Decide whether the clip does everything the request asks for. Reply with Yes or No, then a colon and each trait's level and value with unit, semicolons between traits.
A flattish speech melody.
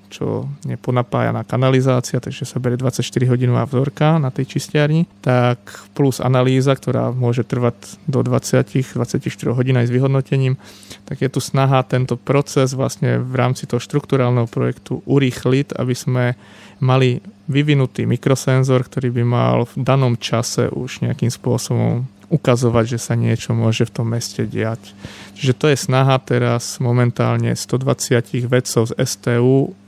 Yes: narrow, 2.1 semitones